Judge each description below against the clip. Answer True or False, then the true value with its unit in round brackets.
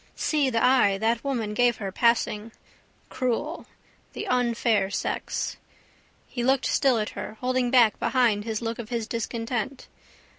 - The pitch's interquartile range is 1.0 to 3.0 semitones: True (2.5 semitones)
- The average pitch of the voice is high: True (235 Hz)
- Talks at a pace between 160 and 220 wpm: False (140 wpm)